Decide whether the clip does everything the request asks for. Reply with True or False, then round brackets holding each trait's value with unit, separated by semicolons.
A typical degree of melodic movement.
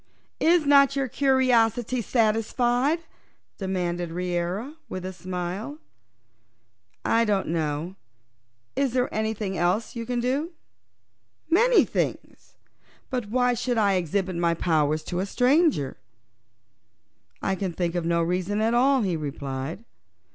False (6.2 semitones)